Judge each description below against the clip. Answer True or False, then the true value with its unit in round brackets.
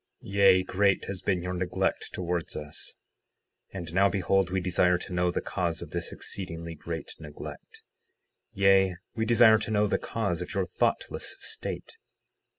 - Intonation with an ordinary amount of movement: False (2.2 semitones)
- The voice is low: True (90 Hz)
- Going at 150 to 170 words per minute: True (160 wpm)